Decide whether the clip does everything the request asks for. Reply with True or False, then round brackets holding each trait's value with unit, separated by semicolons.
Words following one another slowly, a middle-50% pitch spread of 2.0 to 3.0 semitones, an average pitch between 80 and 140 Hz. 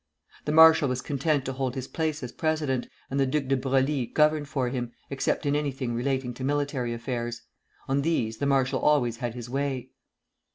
False (190 wpm; 2.6 semitones; 135 Hz)